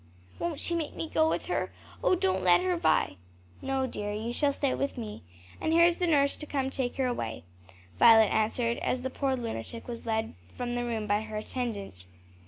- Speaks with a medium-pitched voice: No, high, 240 Hz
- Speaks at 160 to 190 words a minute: No, fast, 205 wpm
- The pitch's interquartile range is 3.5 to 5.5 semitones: Yes, average, 4.6 semitones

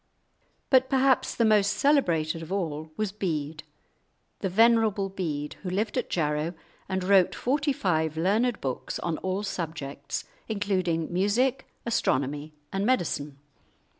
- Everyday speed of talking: No, slow, 130 wpm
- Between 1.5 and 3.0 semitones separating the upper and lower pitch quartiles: No, wide, 5.4 semitones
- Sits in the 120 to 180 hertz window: No, high, 190 Hz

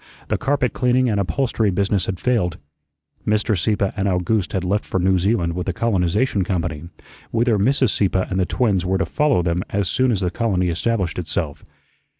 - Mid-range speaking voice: No, low, 100 Hz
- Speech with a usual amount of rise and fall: Yes, average, 4.2 semitones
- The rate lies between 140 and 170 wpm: No, average, 185 wpm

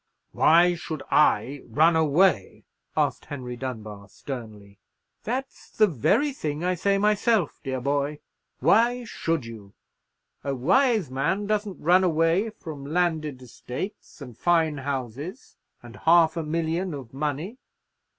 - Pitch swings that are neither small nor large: No, wide, 5.8 semitones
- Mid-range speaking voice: Yes, medium, 155 Hz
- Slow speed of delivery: Yes, slow, 130 wpm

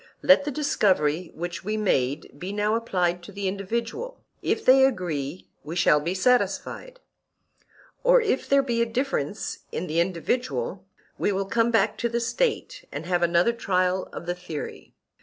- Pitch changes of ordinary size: No, wide, 6.2 semitones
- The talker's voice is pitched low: No, high, 200 Hz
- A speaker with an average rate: Yes, average, 160 wpm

